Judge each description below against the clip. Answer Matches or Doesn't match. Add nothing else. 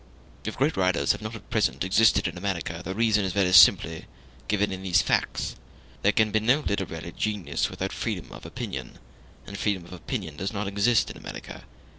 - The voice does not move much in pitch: Doesn't match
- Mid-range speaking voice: Doesn't match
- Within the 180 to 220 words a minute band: Matches